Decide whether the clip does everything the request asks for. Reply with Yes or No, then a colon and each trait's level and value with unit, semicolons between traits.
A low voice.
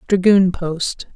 No: medium, 185 Hz